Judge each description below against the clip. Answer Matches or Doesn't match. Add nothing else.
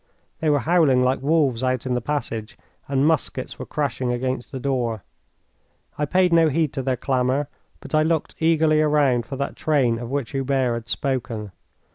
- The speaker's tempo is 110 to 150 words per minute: Doesn't match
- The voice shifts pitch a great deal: Doesn't match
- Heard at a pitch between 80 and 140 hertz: Matches